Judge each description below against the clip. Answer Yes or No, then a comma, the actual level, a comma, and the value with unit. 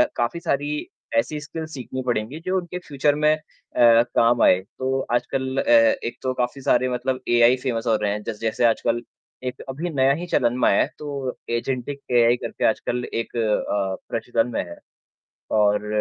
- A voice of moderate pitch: No, low, 125 Hz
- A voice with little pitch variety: No, average, 3.4 semitones